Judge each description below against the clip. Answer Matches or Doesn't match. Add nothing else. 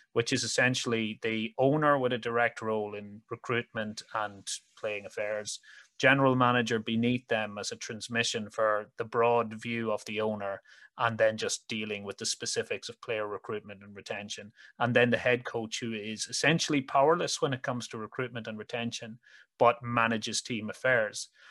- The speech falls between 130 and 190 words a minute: Matches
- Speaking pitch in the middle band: Doesn't match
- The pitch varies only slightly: Matches